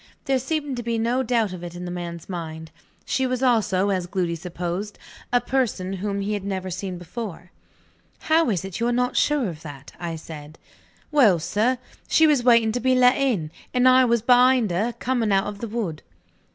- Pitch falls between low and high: No, high, 210 Hz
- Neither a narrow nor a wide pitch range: No, wide, 5.8 semitones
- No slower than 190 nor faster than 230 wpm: Yes, fast, 205 wpm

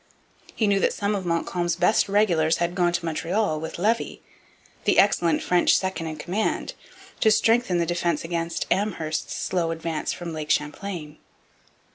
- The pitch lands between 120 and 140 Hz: No, medium, 175 Hz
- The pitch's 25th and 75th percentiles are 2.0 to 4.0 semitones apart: Yes, average, 3.4 semitones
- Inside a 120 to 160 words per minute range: Yes, average, 155 wpm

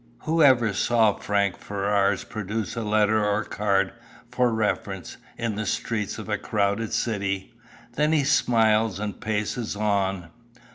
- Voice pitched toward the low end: Yes, low, 105 Hz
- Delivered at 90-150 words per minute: Yes, average, 140 wpm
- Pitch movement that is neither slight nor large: No, narrow, 2.1 semitones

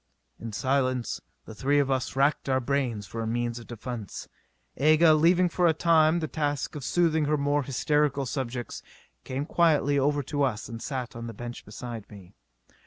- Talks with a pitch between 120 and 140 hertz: Yes, low, 135 Hz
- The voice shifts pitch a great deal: No, average, 3.8 semitones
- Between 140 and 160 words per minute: No, average, 180 wpm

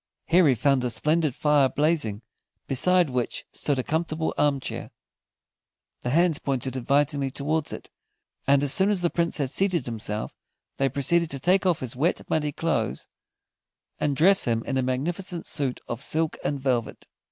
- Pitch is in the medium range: Yes, medium, 145 Hz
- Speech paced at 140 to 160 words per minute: No, average, 170 wpm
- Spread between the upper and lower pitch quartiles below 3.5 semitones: No, average, 4.2 semitones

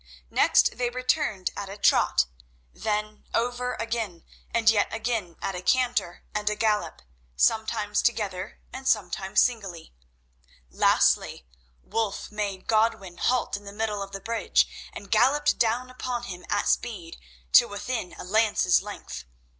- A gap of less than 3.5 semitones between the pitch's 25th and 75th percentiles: Yes, average, 3.1 semitones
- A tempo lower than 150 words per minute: Yes, average, 140 wpm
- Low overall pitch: No, high, 215 Hz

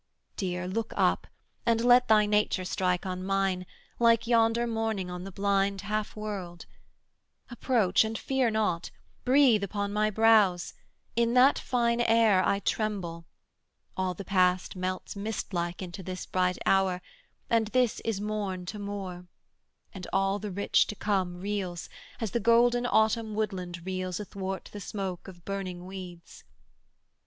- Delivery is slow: No, average, 145 wpm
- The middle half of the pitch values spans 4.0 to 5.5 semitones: No, average, 3.2 semitones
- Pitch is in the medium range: No, high, 200 Hz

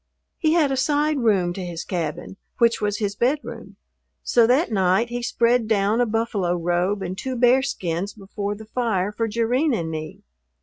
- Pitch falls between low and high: No, high, 220 Hz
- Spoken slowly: No, average, 175 wpm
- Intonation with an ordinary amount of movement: Yes, average, 4.4 semitones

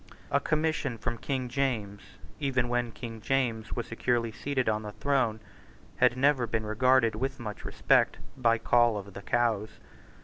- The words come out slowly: No, average, 160 wpm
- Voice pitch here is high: No, low, 120 Hz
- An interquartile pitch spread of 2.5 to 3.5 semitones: Yes, average, 3.0 semitones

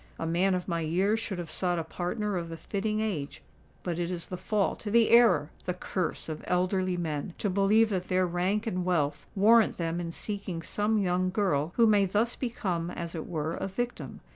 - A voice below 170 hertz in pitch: No, medium, 185 Hz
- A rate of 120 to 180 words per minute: No, average, 195 wpm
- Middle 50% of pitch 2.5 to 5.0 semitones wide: Yes, average, 3.6 semitones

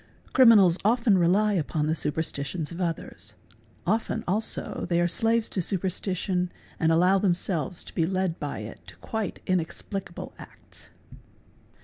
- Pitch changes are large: No, average, 3.5 semitones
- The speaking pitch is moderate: Yes, medium, 180 Hz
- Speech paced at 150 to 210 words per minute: No, slow, 135 wpm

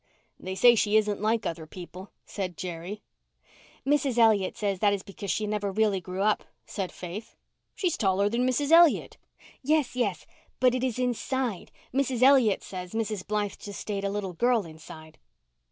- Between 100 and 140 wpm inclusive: No, average, 165 wpm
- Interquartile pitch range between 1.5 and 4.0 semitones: No, average, 4.4 semitones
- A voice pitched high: Yes, high, 210 Hz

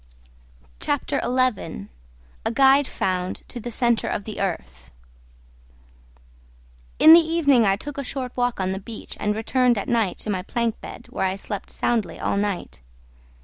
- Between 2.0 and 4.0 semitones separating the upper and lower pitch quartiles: No, average, 4.5 semitones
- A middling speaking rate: Yes, average, 160 wpm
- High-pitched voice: Yes, high, 225 Hz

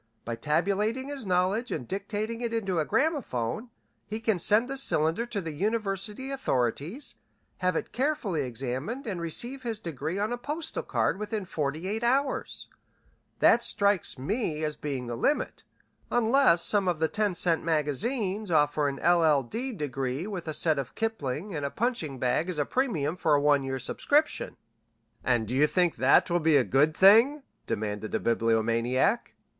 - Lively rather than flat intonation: Yes, wide, 7.7 semitones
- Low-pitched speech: No, medium, 180 Hz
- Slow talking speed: No, average, 170 wpm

